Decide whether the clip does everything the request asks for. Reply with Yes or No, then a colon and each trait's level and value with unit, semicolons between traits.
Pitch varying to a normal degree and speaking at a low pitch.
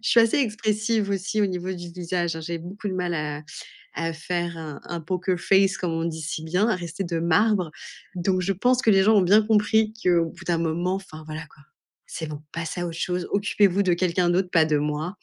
No: average, 3.2 semitones; medium, 180 Hz